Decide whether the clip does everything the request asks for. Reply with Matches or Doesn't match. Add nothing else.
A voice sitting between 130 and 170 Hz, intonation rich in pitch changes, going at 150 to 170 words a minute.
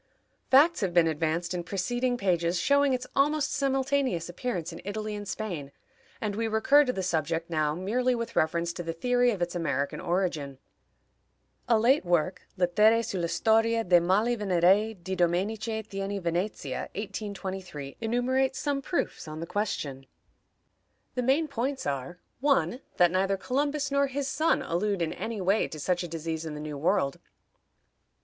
Doesn't match